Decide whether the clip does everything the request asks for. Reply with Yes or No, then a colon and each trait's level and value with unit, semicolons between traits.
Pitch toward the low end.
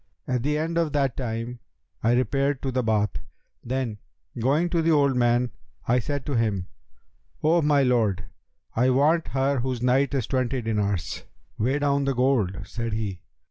Yes: low, 125 Hz